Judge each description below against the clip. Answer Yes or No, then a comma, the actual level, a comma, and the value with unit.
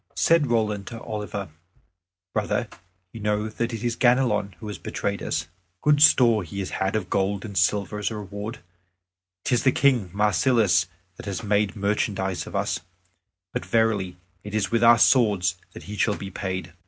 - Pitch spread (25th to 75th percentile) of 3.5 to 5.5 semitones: No, average, 2.9 semitones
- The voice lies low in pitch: Yes, low, 105 Hz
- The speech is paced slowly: No, average, 175 wpm